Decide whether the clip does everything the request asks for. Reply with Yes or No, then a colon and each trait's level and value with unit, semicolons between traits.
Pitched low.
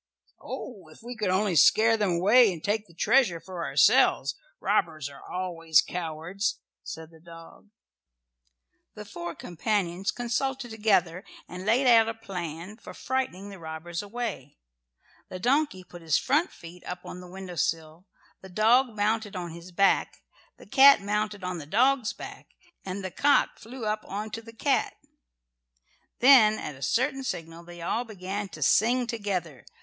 No: high, 195 Hz